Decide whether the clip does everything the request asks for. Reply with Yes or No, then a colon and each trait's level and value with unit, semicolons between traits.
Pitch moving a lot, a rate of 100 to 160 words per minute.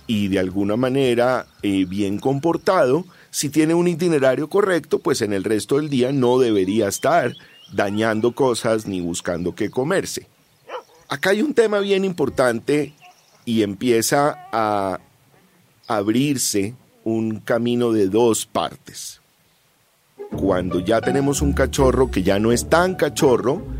Yes: wide, 6.5 semitones; average, 135 wpm